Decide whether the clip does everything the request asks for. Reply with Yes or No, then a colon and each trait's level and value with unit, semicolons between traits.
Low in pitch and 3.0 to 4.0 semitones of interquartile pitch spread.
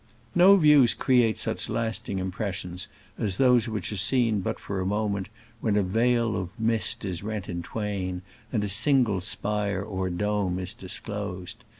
Yes: low, 105 Hz; average, 3.4 semitones